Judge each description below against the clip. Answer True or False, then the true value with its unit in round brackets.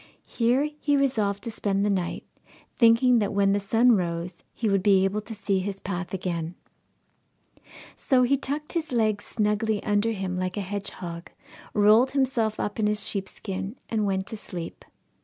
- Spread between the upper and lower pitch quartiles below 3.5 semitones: True (3.1 semitones)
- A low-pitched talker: False (205 Hz)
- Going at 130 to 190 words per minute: True (170 wpm)